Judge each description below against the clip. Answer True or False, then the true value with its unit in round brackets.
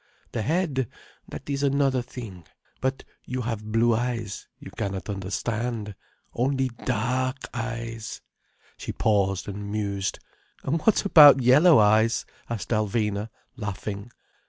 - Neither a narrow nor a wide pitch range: True (3.6 semitones)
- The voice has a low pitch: True (115 Hz)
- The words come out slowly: True (115 wpm)